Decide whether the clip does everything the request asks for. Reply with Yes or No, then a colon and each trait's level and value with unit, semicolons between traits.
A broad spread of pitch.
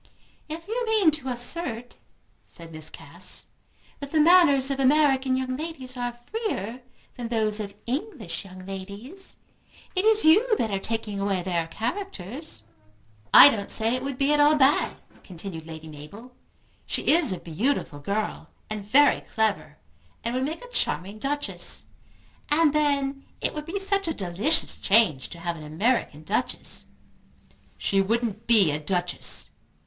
Yes: wide, 7.2 semitones